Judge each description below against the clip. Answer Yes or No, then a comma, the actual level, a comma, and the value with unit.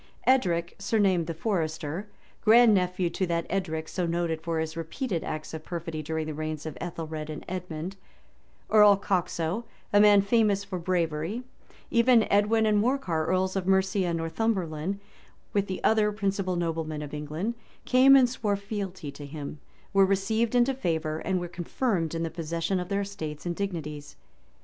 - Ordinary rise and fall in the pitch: Yes, average, 4.0 semitones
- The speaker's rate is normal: Yes, average, 165 wpm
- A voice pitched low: No, medium, 180 Hz